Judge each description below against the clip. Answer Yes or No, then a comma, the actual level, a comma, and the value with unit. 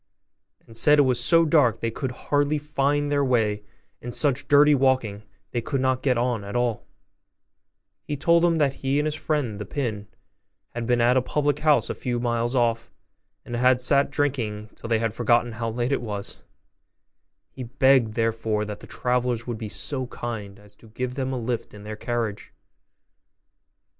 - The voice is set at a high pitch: No, low, 125 Hz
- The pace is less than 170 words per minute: No, average, 190 wpm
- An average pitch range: Yes, average, 3.5 semitones